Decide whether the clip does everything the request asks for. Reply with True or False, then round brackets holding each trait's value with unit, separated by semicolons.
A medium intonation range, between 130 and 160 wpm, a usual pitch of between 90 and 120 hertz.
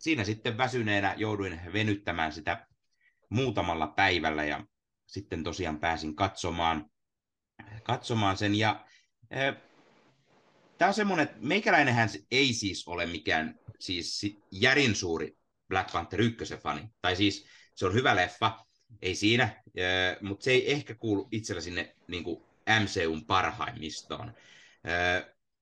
False (4.0 semitones; 120 wpm; 100 Hz)